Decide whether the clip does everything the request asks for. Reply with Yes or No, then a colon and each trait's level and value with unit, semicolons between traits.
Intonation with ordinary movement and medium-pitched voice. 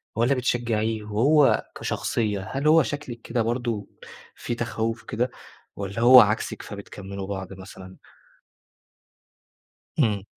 No: average, 3.2 semitones; low, 115 Hz